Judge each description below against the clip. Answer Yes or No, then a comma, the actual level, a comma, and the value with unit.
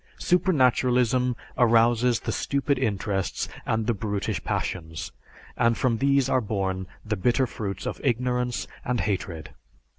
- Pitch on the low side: Yes, low, 120 Hz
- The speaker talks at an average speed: No, slow, 125 wpm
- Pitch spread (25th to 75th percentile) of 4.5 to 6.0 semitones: No, average, 3.6 semitones